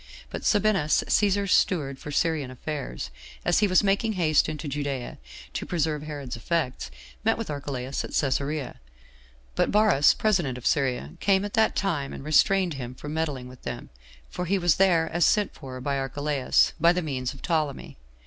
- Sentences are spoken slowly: No, average, 175 wpm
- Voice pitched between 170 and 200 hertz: No, medium, 150 Hz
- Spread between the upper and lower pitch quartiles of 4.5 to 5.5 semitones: Yes, average, 4.9 semitones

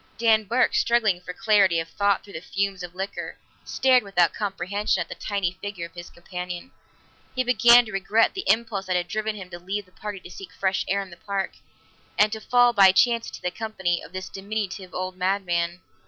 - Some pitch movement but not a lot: Yes, average, 3.1 semitones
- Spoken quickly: Yes, fast, 210 wpm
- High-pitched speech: Yes, high, 195 Hz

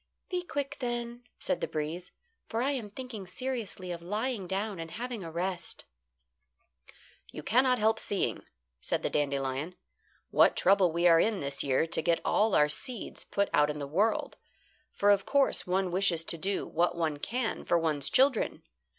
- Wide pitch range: Yes, wide, 6.2 semitones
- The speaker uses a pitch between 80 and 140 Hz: No, high, 190 Hz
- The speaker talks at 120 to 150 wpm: No, average, 175 wpm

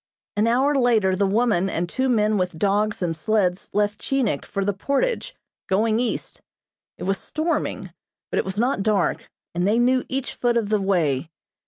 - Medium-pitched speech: No, high, 210 Hz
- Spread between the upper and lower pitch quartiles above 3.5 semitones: Yes, average, 4.2 semitones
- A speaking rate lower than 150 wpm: No, average, 180 wpm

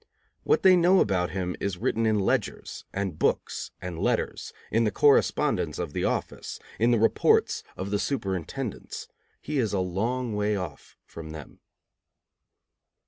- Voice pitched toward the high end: No, low, 105 Hz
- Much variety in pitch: No, average, 4.7 semitones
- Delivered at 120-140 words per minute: No, average, 150 wpm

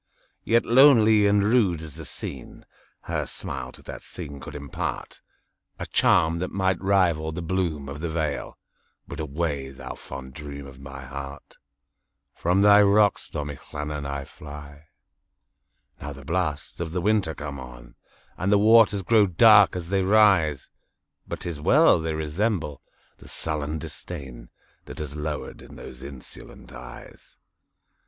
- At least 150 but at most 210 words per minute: No, slow, 135 wpm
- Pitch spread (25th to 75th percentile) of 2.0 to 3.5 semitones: No, average, 5.3 semitones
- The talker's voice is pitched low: Yes, very low, 80 Hz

